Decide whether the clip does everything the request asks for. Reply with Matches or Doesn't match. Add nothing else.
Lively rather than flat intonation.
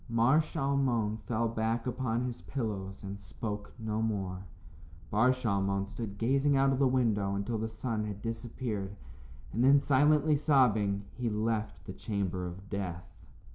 Doesn't match